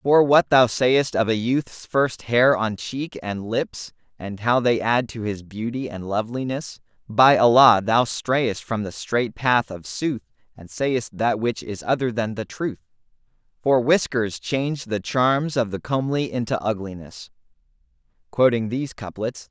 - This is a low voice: Yes, low, 115 Hz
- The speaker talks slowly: No, average, 170 wpm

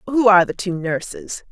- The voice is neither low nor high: No, high, 210 Hz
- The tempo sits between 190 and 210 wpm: Yes, average, 200 wpm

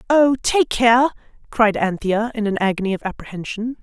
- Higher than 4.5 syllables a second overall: Yes, 5.1 syllables/s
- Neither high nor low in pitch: No, high, 225 Hz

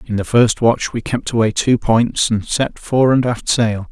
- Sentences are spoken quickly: Yes, fast, 230 wpm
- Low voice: Yes, low, 115 Hz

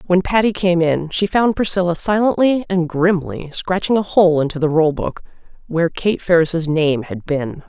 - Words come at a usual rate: Yes, average, 180 wpm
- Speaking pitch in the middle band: Yes, medium, 175 Hz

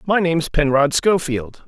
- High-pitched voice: No, medium, 155 Hz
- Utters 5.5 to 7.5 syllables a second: No, 4.5 syllables/s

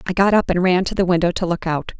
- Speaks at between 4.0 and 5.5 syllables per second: No, 6.4 syllables/s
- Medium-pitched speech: Yes, medium, 180 Hz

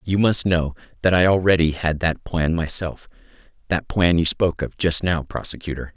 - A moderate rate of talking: Yes, average, 180 wpm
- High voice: No, very low, 85 Hz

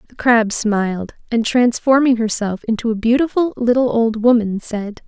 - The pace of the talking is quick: No, average, 155 wpm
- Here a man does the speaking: No, female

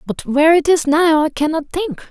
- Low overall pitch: No, very high, 315 Hz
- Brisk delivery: Yes, fast, 230 wpm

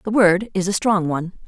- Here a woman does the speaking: Yes, female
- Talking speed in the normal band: No, fast, 245 wpm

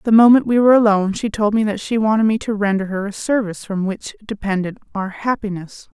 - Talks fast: Yes, fast, 220 wpm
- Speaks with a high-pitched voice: Yes, high, 210 Hz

